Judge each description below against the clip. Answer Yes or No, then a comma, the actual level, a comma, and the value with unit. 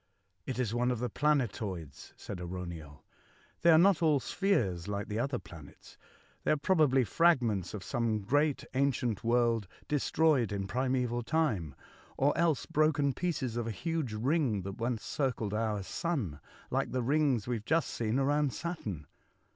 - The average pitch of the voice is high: No, low, 125 Hz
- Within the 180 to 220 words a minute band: No, average, 165 wpm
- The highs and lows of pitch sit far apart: Yes, wide, 5.9 semitones